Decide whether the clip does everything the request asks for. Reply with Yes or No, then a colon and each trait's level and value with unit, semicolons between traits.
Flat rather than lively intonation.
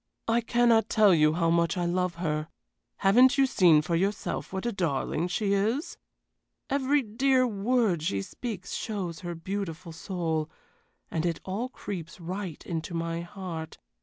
No: average, 4.7 semitones